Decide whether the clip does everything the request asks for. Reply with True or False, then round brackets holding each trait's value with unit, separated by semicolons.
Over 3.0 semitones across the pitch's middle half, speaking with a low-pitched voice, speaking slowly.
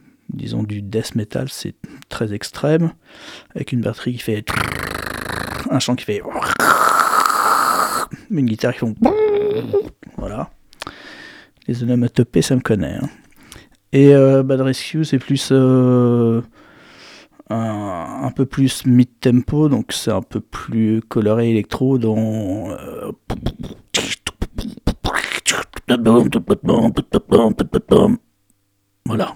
True (3.8 semitones; 125 Hz; 100 wpm)